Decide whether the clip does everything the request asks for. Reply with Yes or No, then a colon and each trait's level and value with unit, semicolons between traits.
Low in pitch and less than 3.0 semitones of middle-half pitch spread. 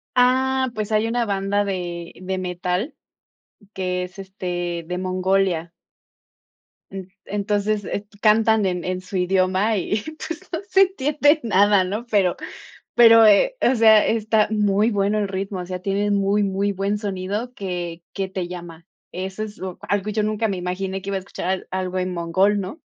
No: high, 195 Hz; narrow, 2.5 semitones